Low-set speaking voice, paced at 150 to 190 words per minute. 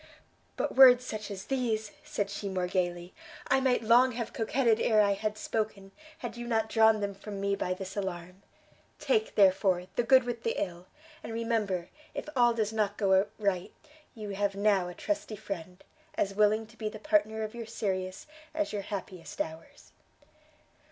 No: high, 210 Hz; average, 180 wpm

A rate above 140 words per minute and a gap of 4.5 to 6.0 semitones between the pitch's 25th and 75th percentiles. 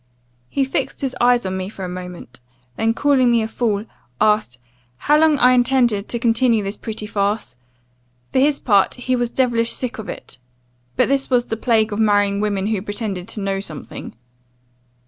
No: average, 185 wpm; average, 3.7 semitones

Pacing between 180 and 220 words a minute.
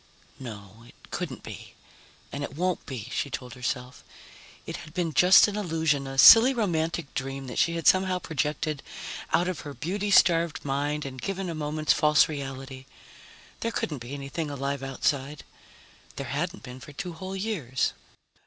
No: average, 165 wpm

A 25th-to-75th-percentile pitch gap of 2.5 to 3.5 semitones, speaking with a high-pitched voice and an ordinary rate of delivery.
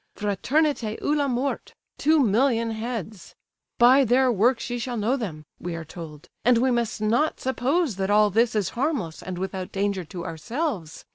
No: average, 5.2 semitones; high, 230 Hz; average, 165 wpm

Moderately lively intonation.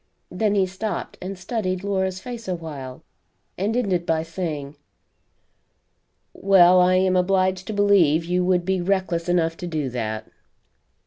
No: narrow, 2.3 semitones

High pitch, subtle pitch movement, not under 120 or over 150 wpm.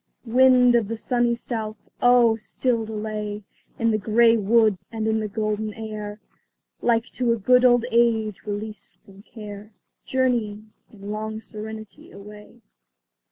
Yes: high, 220 Hz; narrow, 1.8 semitones; average, 140 wpm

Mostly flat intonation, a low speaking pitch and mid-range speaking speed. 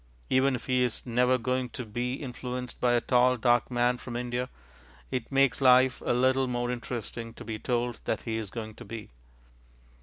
Yes: narrow, 1.2 semitones; low, 125 Hz; average, 190 wpm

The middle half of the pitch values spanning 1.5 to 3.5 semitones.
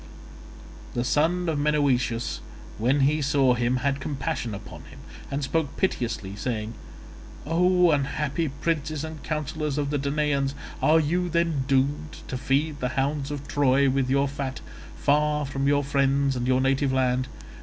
Yes: narrow, 2.4 semitones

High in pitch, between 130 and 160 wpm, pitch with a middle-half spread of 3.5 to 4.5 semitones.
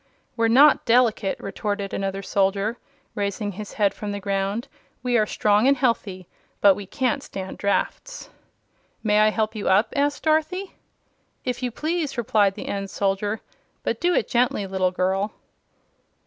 Yes: high, 210 Hz; average, 155 wpm; average, 3.9 semitones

